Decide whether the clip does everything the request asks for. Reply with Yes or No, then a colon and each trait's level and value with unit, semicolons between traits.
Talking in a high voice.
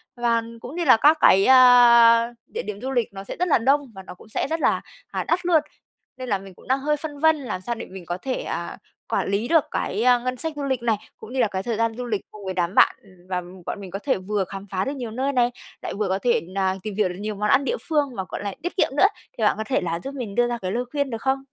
Yes: high, 235 Hz